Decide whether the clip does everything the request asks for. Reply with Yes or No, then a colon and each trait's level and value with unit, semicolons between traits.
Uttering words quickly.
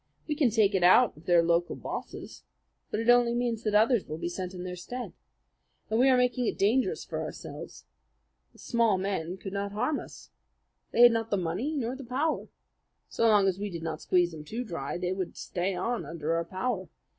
Yes: fast, 215 wpm